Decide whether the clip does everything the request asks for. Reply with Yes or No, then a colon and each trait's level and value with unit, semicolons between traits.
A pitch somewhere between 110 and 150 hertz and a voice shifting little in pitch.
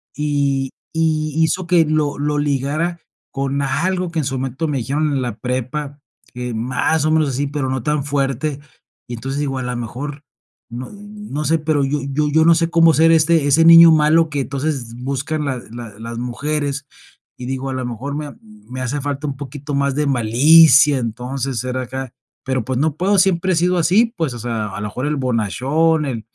No: medium, 140 Hz; average, 3.4 semitones